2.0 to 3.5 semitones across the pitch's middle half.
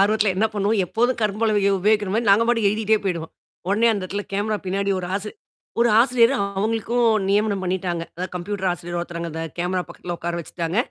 Yes: average, 3.1 semitones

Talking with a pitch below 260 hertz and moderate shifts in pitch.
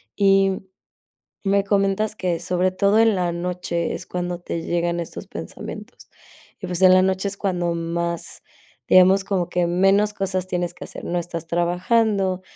No: medium, 185 Hz; narrow, 2.1 semitones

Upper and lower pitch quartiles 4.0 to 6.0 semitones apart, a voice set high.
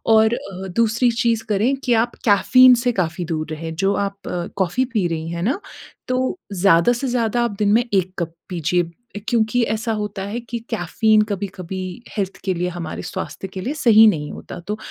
Yes: average, 4.6 semitones; high, 205 Hz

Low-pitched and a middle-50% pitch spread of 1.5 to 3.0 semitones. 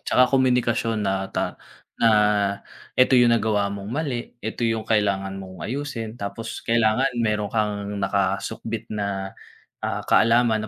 Yes: low, 110 Hz; average, 2.7 semitones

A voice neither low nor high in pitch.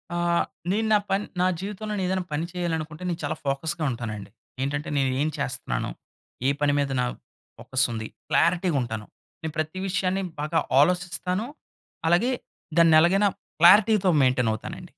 Yes: medium, 165 Hz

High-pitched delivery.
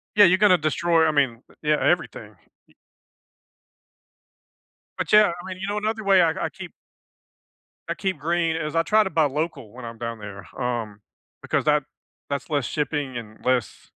No: medium, 150 Hz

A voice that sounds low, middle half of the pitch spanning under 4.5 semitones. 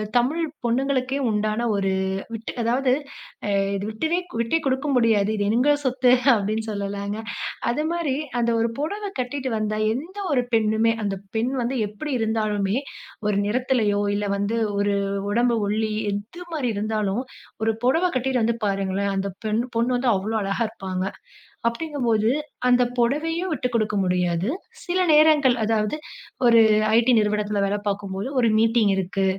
No: high, 225 Hz; average, 3.8 semitones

